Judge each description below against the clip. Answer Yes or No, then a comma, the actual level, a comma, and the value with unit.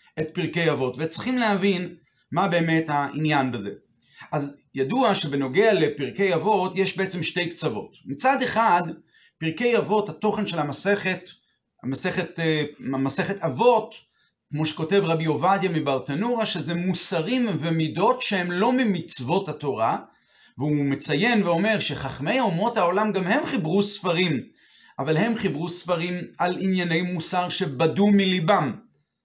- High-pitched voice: No, medium, 175 Hz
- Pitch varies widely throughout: No, average, 4.4 semitones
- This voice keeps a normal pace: Yes, average, 120 wpm